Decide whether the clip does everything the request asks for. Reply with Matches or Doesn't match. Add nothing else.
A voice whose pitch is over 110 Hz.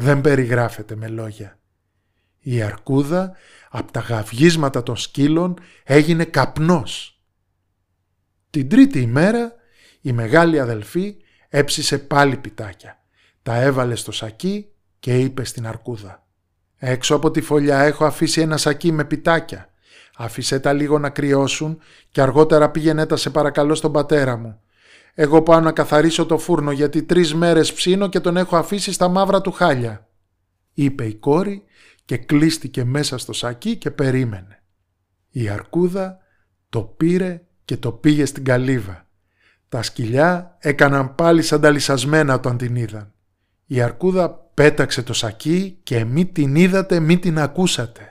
Matches